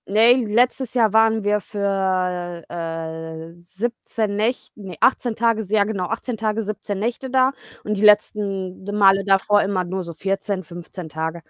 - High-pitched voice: Yes, high, 200 Hz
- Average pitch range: Yes, average, 3.3 semitones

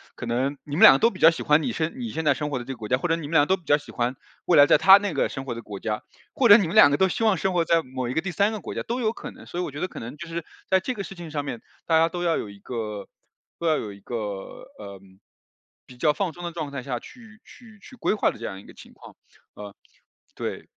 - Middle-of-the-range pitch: Yes, medium, 155 Hz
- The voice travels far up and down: Yes, wide, 6.9 semitones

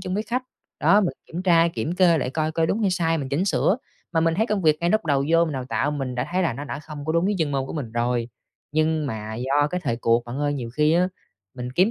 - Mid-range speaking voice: Yes, medium, 155 Hz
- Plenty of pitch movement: No, average, 4.7 semitones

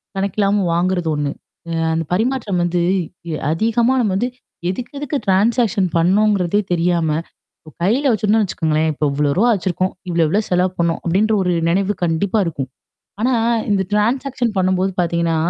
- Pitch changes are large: No, average, 4.2 semitones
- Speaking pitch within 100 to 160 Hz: No, high, 190 Hz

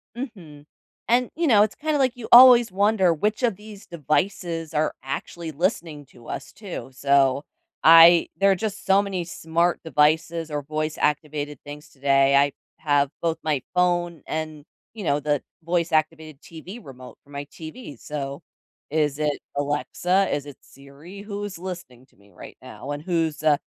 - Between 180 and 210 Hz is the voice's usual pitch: No, medium, 160 Hz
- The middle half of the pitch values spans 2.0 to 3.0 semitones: No, average, 4.8 semitones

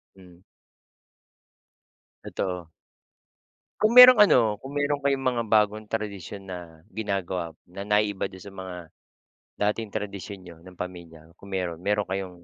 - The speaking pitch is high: No, low, 100 Hz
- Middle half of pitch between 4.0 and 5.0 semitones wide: No, average, 2.9 semitones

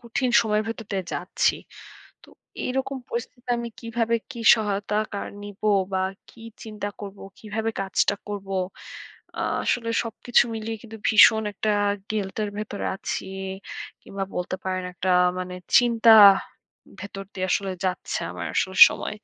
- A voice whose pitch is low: No, high, 210 Hz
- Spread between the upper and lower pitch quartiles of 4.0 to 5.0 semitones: No, average, 2.8 semitones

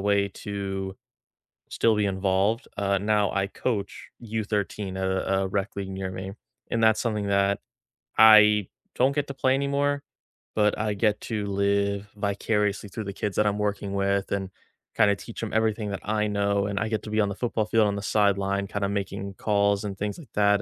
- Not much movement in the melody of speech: Yes, narrow, 1.3 semitones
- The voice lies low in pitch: Yes, low, 100 Hz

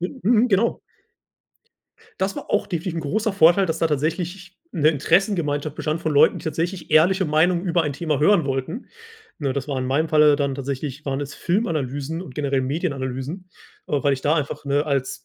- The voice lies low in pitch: No, medium, 155 Hz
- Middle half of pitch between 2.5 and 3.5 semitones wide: No, average, 4.0 semitones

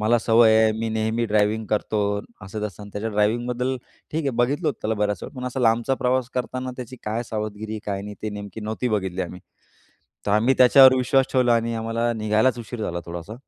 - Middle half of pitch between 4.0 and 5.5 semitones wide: No, average, 2.8 semitones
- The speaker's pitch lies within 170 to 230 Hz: No, low, 110 Hz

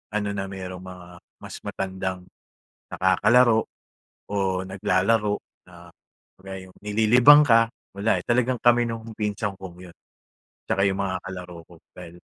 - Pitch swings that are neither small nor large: Yes, average, 3.3 semitones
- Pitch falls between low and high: No, very low, 95 Hz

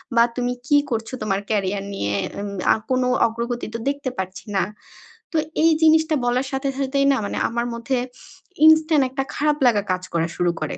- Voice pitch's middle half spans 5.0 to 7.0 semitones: Yes, average, 5.3 semitones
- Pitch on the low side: No, high, 245 Hz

